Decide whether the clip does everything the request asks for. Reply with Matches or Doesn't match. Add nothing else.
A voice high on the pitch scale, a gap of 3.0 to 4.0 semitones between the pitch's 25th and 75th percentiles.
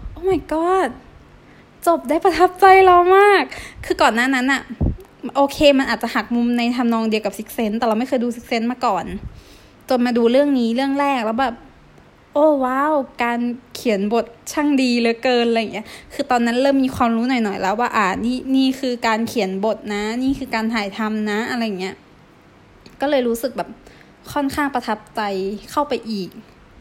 Matches